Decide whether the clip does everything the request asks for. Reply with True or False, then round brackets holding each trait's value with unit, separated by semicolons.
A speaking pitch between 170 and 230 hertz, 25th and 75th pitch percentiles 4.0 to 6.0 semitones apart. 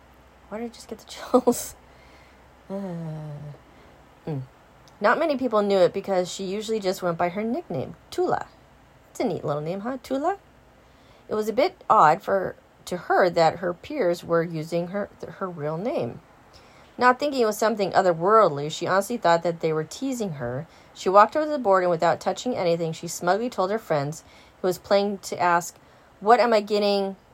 True (185 Hz; 4.8 semitones)